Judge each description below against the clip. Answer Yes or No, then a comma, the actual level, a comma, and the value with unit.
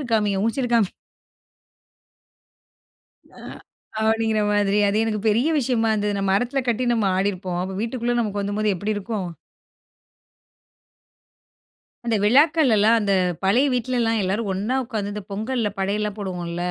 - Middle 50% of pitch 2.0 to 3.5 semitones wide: Yes, average, 2.7 semitones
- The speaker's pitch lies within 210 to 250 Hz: Yes, high, 215 Hz